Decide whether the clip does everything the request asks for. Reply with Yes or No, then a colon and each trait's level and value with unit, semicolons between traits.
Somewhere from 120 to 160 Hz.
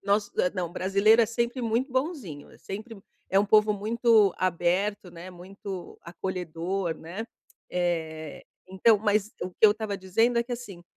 No: high, 200 Hz